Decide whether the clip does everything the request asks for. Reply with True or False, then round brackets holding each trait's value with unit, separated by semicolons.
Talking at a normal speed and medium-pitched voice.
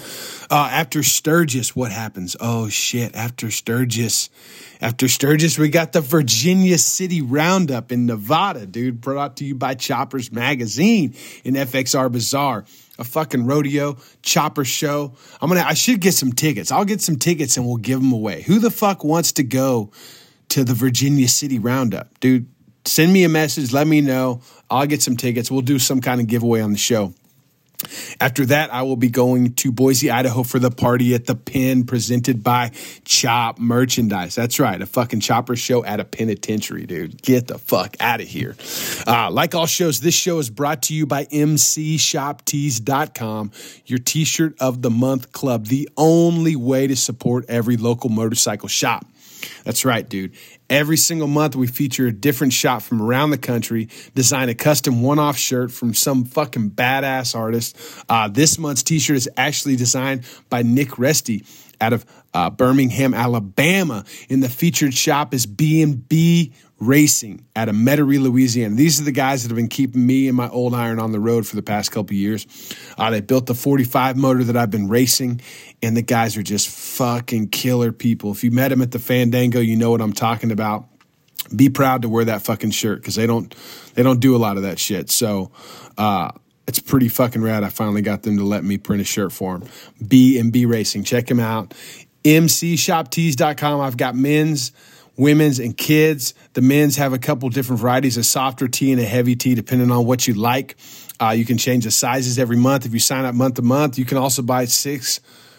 False (195 wpm; 130 Hz)